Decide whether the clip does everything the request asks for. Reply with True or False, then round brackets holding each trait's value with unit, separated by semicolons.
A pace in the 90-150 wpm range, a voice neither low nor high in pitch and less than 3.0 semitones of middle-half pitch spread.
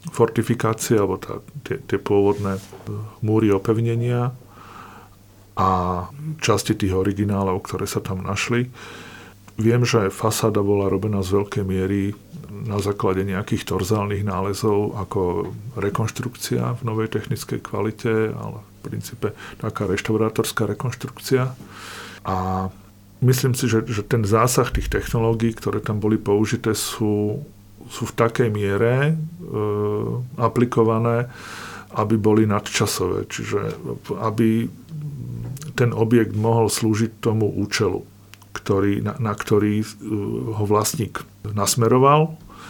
False (110 wpm; 110 Hz; 2.6 semitones)